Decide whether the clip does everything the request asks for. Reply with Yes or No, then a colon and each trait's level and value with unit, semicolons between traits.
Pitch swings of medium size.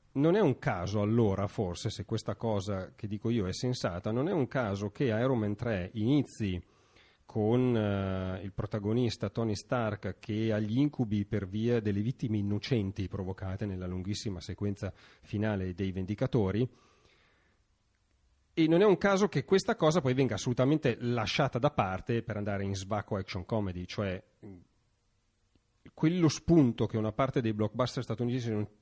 Yes: average, 3.9 semitones